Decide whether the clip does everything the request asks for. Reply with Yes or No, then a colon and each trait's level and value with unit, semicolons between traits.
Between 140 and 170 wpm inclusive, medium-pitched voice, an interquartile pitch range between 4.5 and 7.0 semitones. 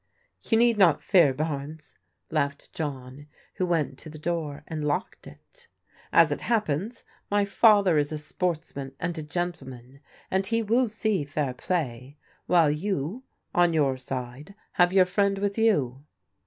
Yes: average, 155 wpm; medium, 160 Hz; wide, 5.6 semitones